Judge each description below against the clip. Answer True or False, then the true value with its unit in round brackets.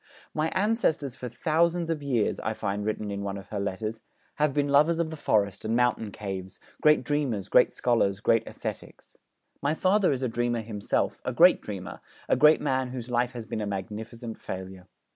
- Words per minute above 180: True (190 wpm)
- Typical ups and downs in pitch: False (6.0 semitones)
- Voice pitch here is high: False (120 Hz)